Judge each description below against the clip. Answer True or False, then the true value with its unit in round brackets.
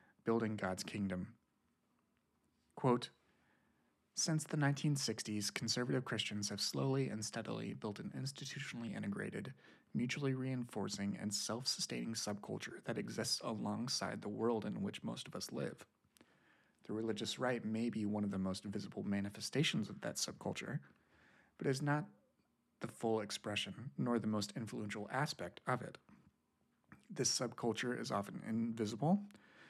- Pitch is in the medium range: False (110 Hz)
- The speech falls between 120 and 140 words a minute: True (135 wpm)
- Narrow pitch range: False (3.9 semitones)